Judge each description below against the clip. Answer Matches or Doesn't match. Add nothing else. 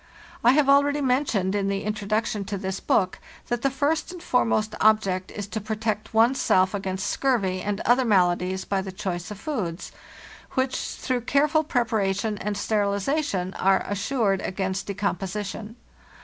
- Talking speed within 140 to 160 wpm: Matches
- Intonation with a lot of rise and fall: Doesn't match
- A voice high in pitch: Matches